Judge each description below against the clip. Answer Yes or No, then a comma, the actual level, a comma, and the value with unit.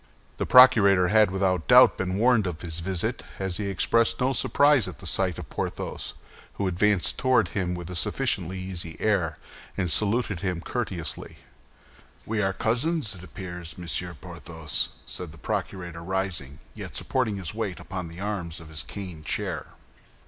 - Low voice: Yes, very low, 95 Hz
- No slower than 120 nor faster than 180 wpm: Yes, average, 165 wpm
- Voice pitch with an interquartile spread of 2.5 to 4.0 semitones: Yes, average, 3.3 semitones